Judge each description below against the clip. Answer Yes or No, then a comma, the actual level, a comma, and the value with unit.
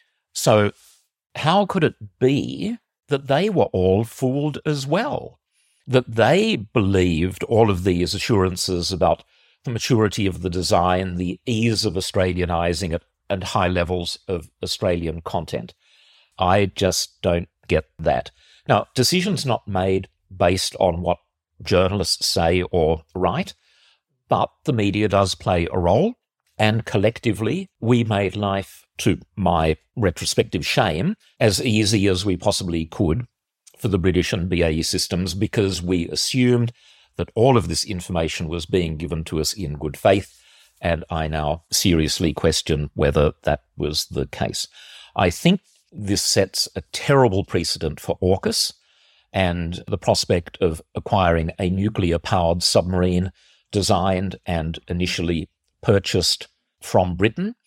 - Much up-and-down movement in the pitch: No, average, 4.2 semitones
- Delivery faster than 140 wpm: No, slow, 135 wpm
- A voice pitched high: No, very low, 95 Hz